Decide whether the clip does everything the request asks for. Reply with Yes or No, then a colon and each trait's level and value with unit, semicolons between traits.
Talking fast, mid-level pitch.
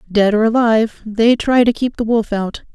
No: fast, 220 wpm; high, 225 Hz